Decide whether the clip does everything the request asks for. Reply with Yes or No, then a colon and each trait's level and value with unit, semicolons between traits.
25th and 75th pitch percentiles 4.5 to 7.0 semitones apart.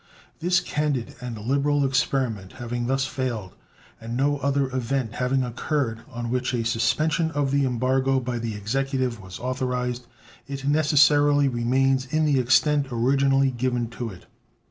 No: average, 2.7 semitones